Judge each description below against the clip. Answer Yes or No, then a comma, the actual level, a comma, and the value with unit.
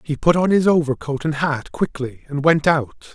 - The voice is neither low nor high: Yes, medium, 150 Hz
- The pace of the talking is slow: No, fast, 210 wpm